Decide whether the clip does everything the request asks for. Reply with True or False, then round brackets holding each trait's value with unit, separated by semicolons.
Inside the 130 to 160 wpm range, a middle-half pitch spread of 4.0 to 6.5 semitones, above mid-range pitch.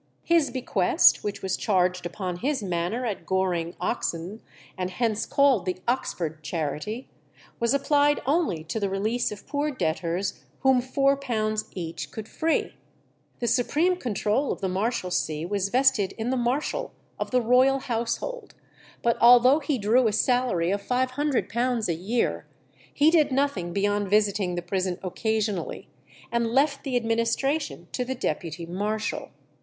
True (145 wpm; 5.6 semitones; 225 Hz)